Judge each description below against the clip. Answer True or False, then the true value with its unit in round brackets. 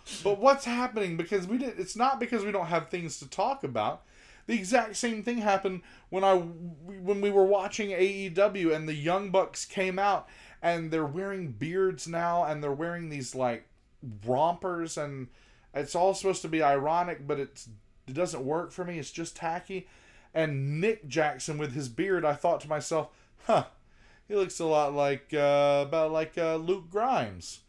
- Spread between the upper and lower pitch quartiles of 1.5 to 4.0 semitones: False (4.6 semitones)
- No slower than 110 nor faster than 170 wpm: False (180 wpm)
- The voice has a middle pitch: True (170 Hz)